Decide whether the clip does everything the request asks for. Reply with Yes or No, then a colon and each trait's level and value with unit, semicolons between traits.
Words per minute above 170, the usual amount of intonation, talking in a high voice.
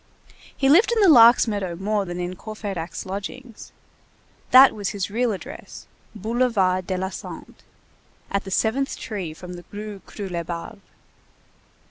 No: average, 140 wpm; average, 4.1 semitones; high, 205 Hz